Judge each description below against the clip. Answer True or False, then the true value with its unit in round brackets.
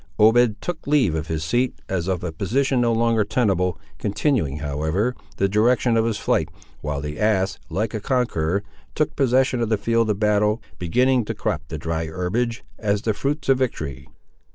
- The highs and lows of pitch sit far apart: True (5.8 semitones)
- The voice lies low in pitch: True (105 Hz)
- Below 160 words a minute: False (180 wpm)